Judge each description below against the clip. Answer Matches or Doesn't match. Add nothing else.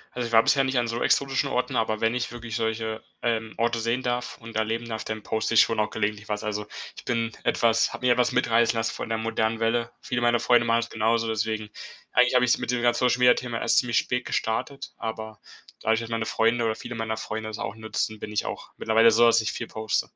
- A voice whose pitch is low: Matches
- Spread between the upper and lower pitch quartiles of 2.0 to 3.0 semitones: Doesn't match